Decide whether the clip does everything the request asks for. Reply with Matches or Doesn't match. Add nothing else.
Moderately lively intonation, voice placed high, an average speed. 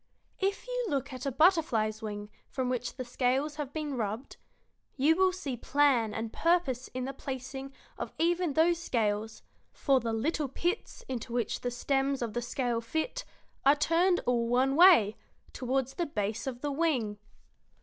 Matches